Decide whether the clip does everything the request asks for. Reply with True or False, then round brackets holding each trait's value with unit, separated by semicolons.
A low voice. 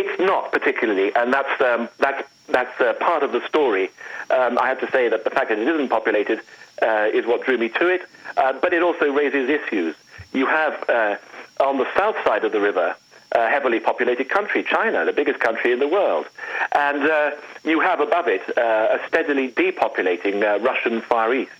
False (385 Hz)